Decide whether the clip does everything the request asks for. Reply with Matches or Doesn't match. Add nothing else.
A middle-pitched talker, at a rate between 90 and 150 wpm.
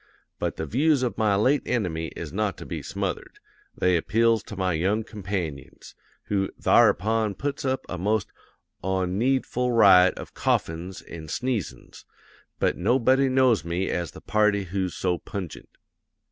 Doesn't match